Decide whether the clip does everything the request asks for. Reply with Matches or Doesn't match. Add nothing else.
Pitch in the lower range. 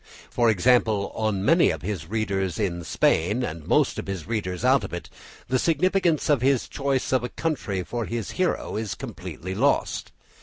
Matches